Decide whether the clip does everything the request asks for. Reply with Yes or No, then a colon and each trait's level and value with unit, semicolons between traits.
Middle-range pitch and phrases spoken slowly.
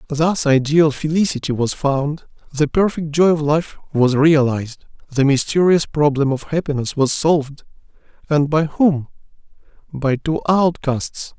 Yes: medium, 150 Hz; slow, 130 wpm